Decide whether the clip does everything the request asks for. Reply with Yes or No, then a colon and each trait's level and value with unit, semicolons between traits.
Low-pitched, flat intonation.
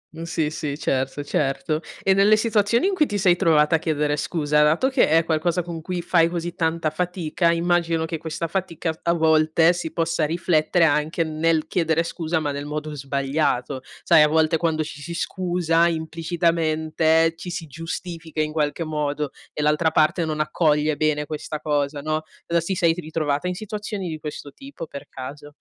No: medium, 160 Hz; narrow, 2.0 semitones